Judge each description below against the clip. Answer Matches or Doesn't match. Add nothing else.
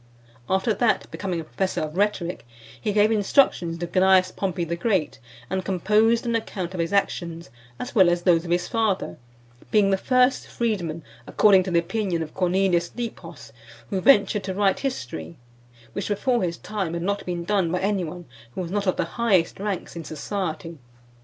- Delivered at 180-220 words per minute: Matches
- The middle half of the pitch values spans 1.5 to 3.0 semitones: Doesn't match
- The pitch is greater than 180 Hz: Matches